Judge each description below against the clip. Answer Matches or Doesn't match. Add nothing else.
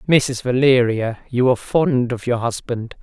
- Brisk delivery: Doesn't match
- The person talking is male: Doesn't match